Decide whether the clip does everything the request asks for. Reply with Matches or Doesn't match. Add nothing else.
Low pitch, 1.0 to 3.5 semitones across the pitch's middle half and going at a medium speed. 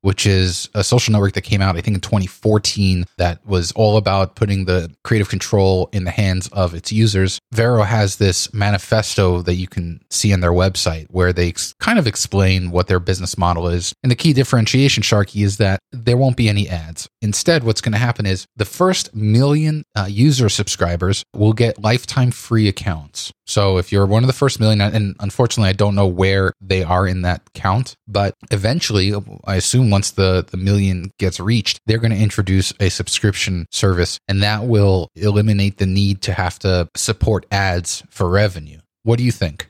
Matches